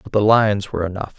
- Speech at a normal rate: No, fast, 250 wpm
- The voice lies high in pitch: No, low, 100 Hz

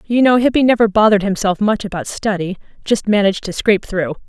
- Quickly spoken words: No, average, 195 wpm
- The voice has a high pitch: Yes, high, 205 Hz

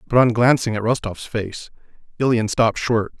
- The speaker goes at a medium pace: Yes, average, 170 wpm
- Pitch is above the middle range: No, low, 115 Hz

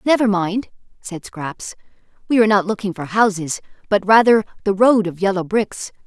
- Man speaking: No, female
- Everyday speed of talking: Yes, average, 170 wpm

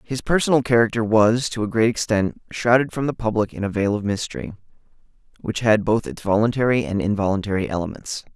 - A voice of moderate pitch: No, low, 110 Hz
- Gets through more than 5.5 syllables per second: Yes, 6.0 syllables/s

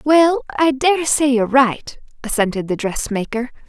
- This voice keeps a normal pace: Yes, average, 145 wpm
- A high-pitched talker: Yes, very high, 260 Hz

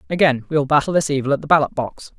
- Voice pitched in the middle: Yes, medium, 145 Hz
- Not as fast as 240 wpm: No, fast, 275 wpm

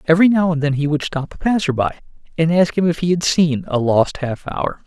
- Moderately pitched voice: Yes, medium, 160 Hz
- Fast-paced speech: Yes, fast, 260 wpm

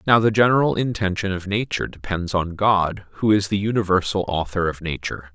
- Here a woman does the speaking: No, male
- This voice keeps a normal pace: Yes, average, 180 wpm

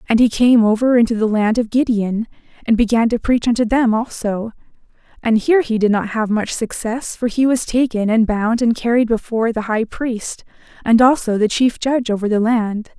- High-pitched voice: Yes, high, 230 Hz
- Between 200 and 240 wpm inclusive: Yes, fast, 205 wpm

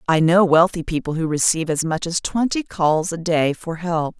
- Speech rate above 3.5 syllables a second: Yes, 5.0 syllables/s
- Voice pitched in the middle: Yes, medium, 165 Hz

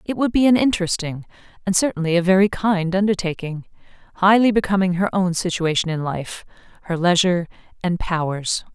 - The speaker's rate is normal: Yes, average, 150 wpm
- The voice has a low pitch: No, medium, 185 Hz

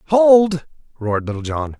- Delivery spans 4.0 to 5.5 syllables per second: Yes, 4.9 syllables/s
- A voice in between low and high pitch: Yes, medium, 150 Hz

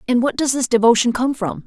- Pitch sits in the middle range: No, high, 245 Hz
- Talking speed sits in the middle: No, fast, 250 wpm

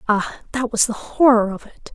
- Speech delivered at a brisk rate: Yes, fast, 215 wpm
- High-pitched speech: Yes, high, 230 Hz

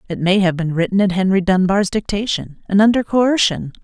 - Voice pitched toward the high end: Yes, high, 195 Hz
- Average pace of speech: Yes, average, 190 wpm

